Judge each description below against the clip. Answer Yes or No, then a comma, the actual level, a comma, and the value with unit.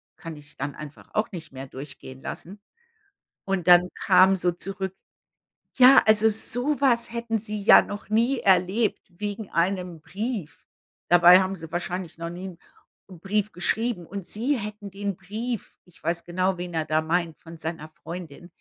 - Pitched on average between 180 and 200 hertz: Yes, medium, 185 Hz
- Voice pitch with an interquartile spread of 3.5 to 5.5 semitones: Yes, average, 4.0 semitones